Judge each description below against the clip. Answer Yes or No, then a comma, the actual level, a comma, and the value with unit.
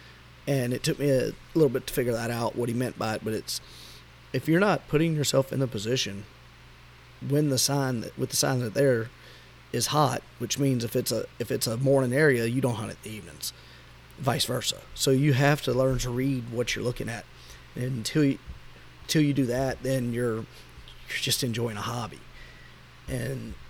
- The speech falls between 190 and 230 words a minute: Yes, fast, 205 wpm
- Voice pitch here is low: Yes, low, 125 Hz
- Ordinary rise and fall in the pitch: Yes, average, 3.8 semitones